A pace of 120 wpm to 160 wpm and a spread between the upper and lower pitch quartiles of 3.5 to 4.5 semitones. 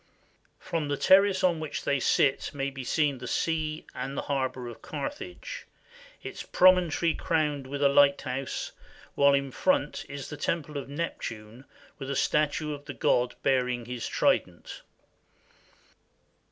No: average, 145 wpm; average, 3.0 semitones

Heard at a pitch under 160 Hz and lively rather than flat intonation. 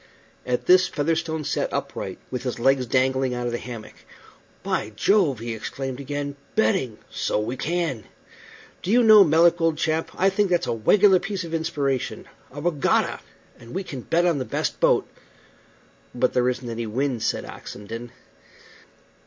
Yes: medium, 140 Hz; wide, 5.8 semitones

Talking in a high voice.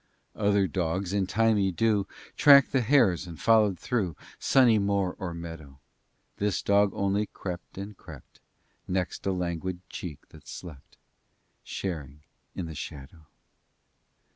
No: very low, 95 Hz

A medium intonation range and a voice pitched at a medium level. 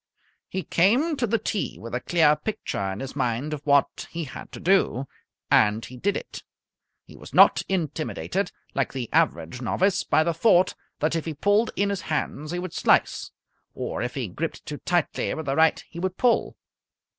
No: wide, 5.9 semitones; medium, 160 Hz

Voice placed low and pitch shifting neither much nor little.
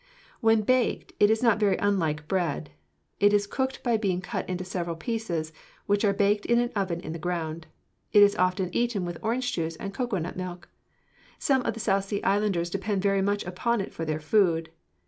No: high, 195 Hz; average, 3.5 semitones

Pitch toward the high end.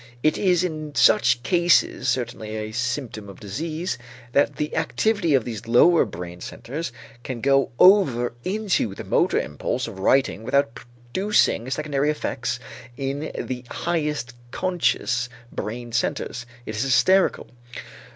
No: low, 135 Hz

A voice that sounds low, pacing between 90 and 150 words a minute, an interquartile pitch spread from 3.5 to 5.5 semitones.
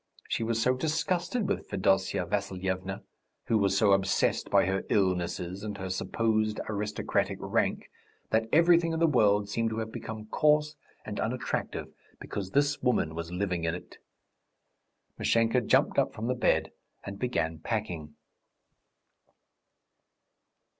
Yes: low, 105 Hz; slow, 135 wpm; average, 4.6 semitones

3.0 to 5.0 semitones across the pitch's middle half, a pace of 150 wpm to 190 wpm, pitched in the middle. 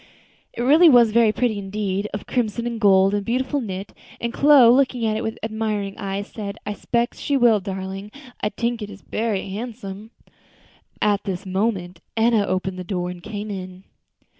No: average, 3.3 semitones; average, 175 wpm; high, 210 Hz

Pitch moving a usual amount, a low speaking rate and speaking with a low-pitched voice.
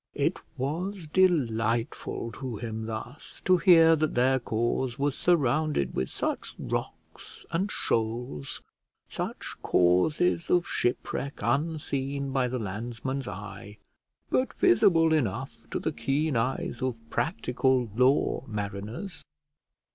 No: wide, 5.7 semitones; slow, 115 wpm; low, 130 Hz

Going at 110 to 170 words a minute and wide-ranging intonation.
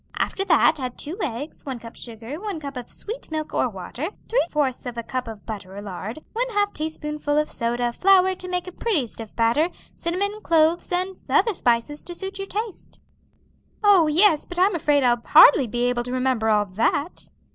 No: average, 200 wpm; wide, 7.2 semitones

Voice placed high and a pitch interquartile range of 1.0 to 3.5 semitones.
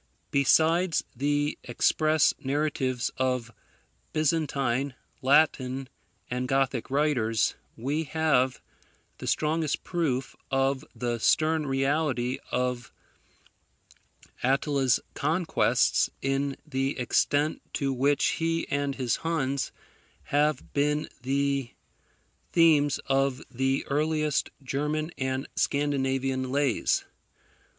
No: medium, 140 Hz; narrow, 2.5 semitones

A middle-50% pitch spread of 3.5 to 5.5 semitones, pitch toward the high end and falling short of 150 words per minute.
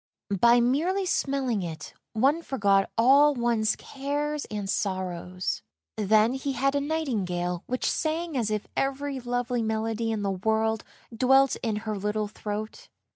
Yes: average, 4.7 semitones; high, 230 Hz; average, 140 wpm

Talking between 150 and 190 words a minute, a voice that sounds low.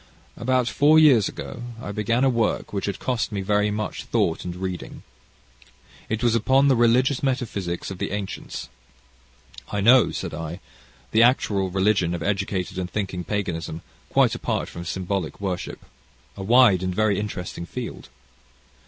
Yes: average, 155 wpm; low, 105 Hz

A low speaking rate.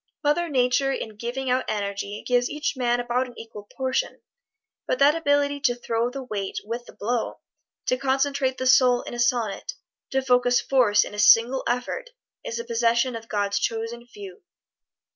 No: average, 175 wpm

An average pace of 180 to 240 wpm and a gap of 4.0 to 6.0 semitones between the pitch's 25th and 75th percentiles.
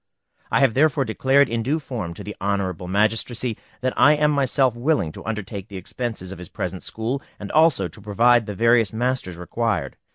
Yes: average, 190 wpm; average, 4.7 semitones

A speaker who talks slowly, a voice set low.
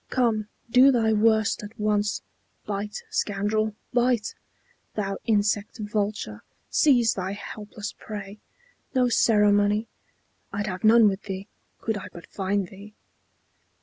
No: slow, 120 wpm; high, 210 Hz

